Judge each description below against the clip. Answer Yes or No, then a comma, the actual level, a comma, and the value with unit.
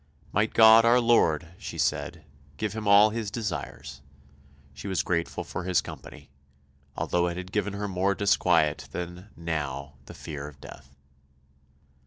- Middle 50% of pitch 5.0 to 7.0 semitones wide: Yes, wide, 5.4 semitones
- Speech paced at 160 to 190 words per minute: No, average, 150 wpm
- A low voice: Yes, very low, 90 Hz